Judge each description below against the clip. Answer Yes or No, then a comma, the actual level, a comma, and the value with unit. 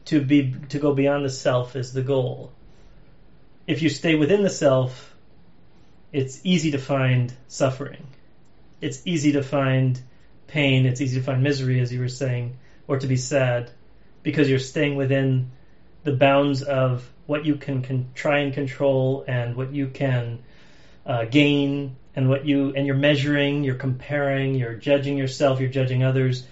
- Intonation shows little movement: Yes, narrow, 1.6 semitones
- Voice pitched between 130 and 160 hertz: Yes, low, 135 Hz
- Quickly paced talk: No, average, 165 wpm